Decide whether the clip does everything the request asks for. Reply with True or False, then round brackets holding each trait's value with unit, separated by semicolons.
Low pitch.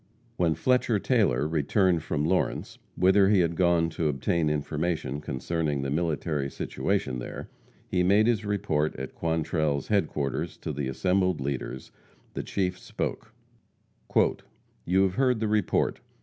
True (85 Hz)